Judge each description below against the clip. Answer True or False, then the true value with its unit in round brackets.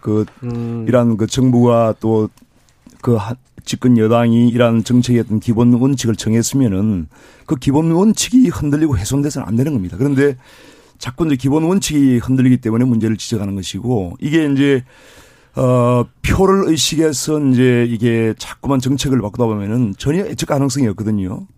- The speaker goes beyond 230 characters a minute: True (335 characters per minute)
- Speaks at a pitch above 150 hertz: False (125 Hz)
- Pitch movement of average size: True (3.6 semitones)